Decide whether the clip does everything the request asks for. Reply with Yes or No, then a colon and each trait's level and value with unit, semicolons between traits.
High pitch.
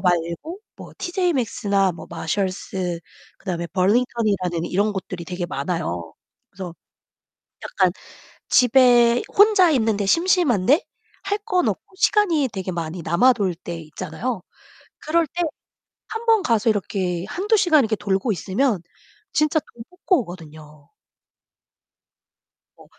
Yes: high, 210 Hz